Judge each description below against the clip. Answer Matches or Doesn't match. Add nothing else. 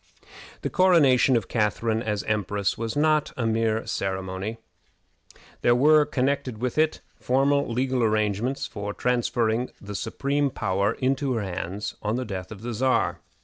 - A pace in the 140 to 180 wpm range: Matches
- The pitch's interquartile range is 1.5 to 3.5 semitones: Doesn't match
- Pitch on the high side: Doesn't match